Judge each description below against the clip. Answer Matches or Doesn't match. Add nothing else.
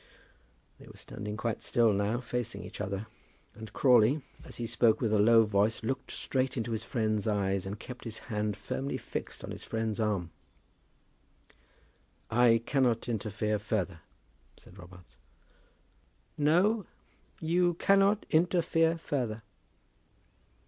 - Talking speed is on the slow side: Matches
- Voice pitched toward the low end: Matches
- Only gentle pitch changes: Doesn't match